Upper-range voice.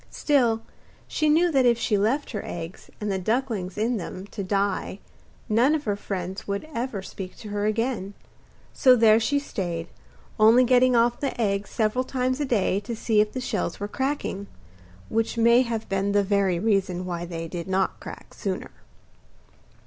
Yes: high, 215 Hz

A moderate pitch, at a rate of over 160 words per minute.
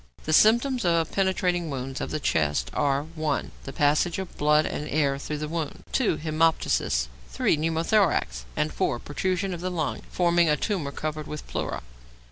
Yes: medium, 155 Hz; average, 170 wpm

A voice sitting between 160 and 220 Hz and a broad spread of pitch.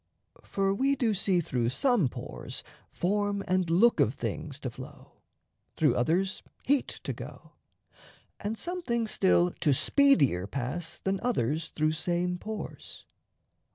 Yes: medium, 185 Hz; wide, 5.8 semitones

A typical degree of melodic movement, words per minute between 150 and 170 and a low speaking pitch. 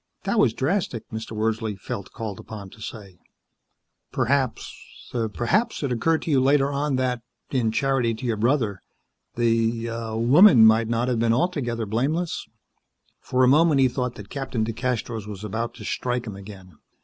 Yes: average, 3.4 semitones; average, 165 wpm; low, 115 Hz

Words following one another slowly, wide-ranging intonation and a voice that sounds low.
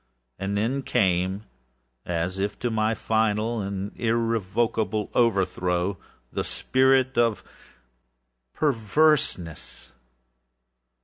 No: slow, 80 wpm; average, 3.4 semitones; low, 110 Hz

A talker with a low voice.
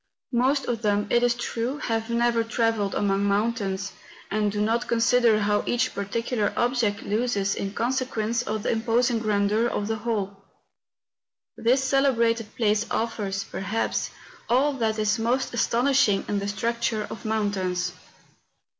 No: high, 225 Hz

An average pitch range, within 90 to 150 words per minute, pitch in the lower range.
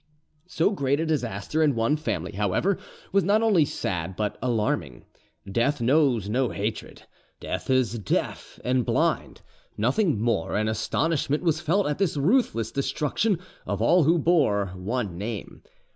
No: wide, 7.1 semitones; average, 145 wpm; low, 130 Hz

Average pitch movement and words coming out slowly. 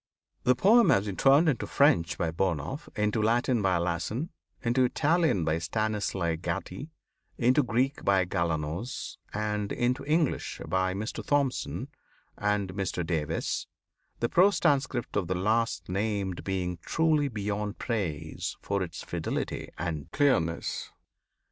No: wide, 6.3 semitones; slow, 130 wpm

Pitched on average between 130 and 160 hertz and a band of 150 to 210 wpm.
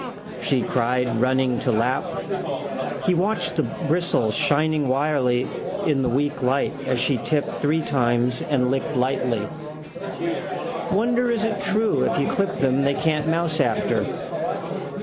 No: medium, 140 Hz; average, 140 wpm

